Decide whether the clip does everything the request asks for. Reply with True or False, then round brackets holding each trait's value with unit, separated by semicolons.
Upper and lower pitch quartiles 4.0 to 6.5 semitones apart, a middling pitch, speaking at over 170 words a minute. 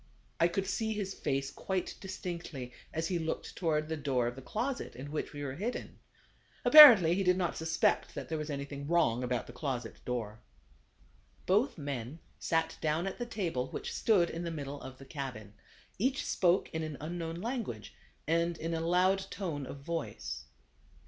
True (5.0 semitones; 160 Hz; 180 wpm)